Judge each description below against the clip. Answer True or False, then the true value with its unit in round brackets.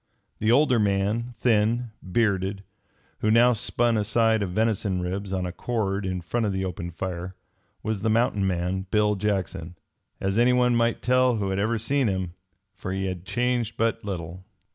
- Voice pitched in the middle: False (105 Hz)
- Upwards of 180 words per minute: False (175 wpm)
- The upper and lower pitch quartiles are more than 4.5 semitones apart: False (3.6 semitones)